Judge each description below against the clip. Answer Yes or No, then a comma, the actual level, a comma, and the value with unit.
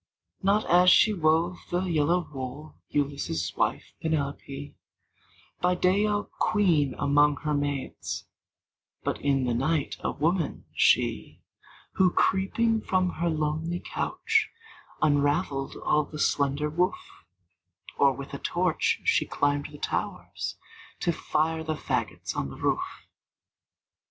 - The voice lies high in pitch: No, medium, 155 Hz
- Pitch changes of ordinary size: Yes, average, 3.9 semitones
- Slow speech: Yes, slow, 125 wpm